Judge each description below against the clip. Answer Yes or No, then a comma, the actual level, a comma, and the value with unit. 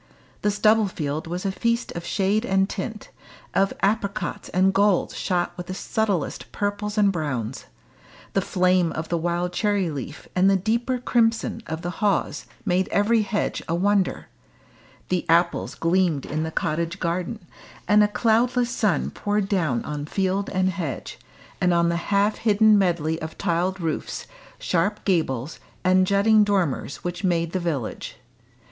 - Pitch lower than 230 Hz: Yes, medium, 185 Hz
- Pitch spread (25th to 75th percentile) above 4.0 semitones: No, average, 3.4 semitones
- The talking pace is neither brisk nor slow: Yes, average, 155 wpm